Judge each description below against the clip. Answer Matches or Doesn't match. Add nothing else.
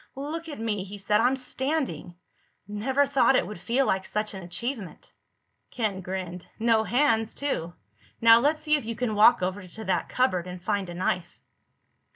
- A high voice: Matches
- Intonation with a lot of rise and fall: Matches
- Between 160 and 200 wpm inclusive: Matches